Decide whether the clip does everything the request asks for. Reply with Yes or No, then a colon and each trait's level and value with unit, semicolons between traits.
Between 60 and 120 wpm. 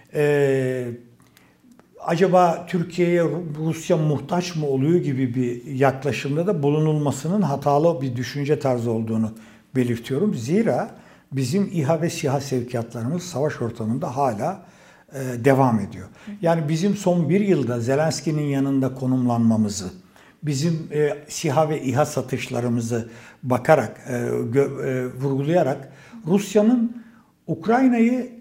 Yes: slow, 95 wpm